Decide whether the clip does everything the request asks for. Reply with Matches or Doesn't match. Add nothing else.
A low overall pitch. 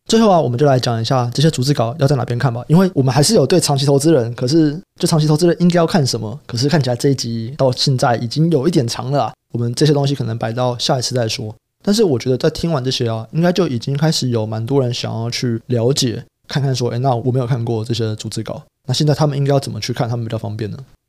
Matches